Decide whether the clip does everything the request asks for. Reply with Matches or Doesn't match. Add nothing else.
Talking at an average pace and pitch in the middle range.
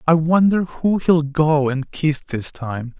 Matches